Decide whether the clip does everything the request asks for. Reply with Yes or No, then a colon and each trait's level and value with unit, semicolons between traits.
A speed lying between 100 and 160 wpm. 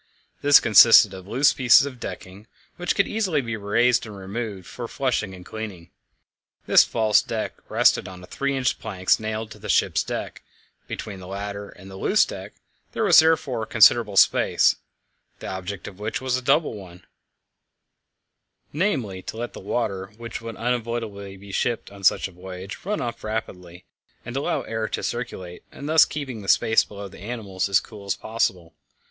No: average, 180 wpm